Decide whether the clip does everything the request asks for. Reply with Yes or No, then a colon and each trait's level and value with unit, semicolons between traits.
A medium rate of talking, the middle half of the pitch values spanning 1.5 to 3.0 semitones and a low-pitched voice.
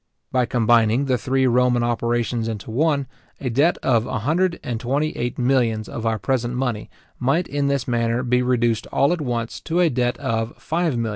Yes: average, 190 wpm; average, 2.7 semitones; low, 125 Hz